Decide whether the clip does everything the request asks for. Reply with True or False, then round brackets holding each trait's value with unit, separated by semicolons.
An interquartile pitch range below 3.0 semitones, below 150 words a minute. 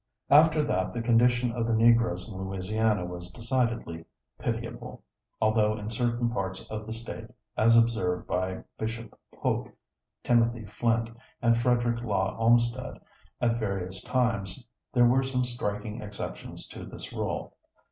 True (2.6 semitones; 140 wpm)